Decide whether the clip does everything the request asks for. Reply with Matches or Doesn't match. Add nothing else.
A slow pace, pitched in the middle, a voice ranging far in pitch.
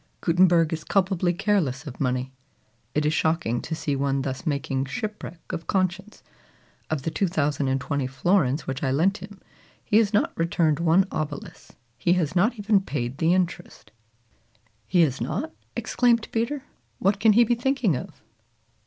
Doesn't match